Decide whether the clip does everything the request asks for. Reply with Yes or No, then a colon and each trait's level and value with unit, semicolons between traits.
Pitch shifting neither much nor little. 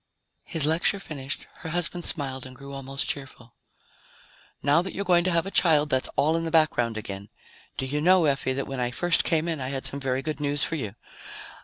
Yes: average, 3.8 semitones